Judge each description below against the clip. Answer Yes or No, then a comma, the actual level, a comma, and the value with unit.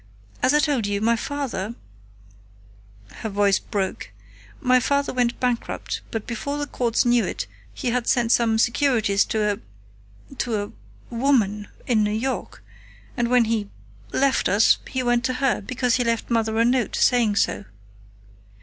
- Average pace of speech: Yes, average, 160 wpm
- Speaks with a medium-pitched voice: No, high, 235 Hz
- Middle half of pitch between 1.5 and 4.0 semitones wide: Yes, average, 2.8 semitones